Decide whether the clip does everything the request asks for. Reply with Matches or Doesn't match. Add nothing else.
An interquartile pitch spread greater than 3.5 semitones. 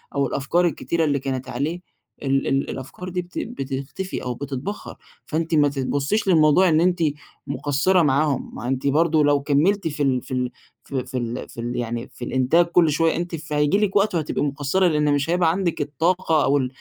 Matches